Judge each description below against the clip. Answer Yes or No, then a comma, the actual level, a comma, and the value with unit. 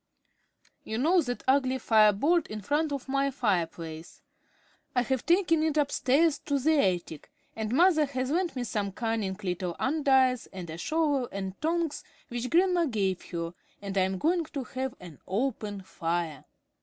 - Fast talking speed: No, average, 165 wpm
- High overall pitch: Yes, very high, 255 Hz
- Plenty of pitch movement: Yes, wide, 7.5 semitones